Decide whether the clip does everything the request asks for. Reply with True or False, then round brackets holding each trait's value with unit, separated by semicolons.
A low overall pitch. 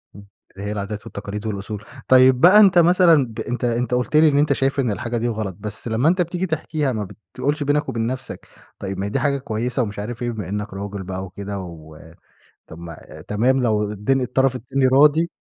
True (120 Hz)